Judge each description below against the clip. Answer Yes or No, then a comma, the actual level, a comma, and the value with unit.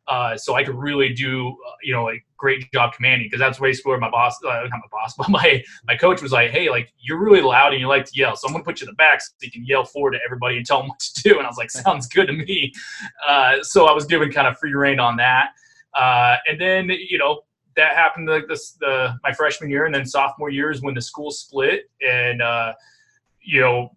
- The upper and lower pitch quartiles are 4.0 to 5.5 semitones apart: Yes, average, 4.5 semitones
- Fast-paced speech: Yes, fast, 265 wpm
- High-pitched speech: No, medium, 140 Hz